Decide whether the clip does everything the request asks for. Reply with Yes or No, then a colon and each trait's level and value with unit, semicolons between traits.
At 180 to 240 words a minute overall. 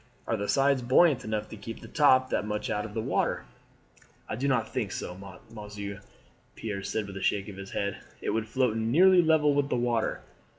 Yes: fast, 205 wpm